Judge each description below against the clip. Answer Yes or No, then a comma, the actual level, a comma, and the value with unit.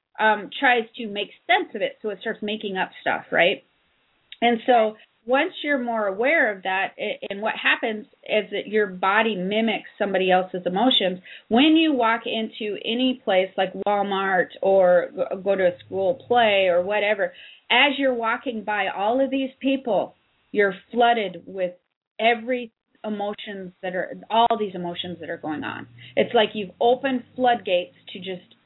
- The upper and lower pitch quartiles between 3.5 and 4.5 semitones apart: Yes, average, 4.0 semitones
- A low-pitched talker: No, high, 215 Hz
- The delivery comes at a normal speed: Yes, average, 165 wpm